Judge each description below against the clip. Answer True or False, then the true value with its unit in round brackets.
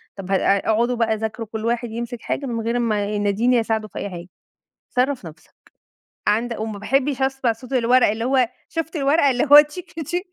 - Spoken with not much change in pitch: False (3.5 semitones)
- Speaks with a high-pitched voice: True (235 Hz)